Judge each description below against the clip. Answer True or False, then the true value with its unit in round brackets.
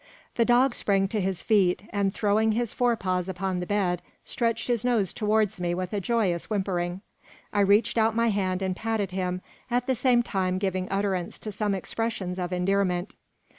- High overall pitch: True (200 Hz)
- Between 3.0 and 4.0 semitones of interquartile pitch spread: True (3.3 semitones)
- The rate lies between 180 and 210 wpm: True (185 wpm)